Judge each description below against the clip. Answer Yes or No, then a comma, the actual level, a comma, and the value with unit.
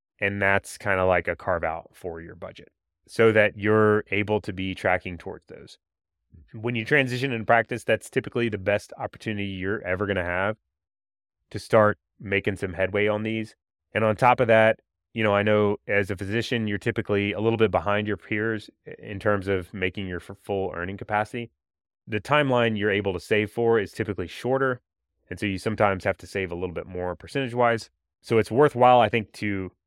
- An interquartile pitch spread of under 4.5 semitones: Yes, narrow, 2.6 semitones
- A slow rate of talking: No, average, 200 wpm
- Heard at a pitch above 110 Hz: No, low, 105 Hz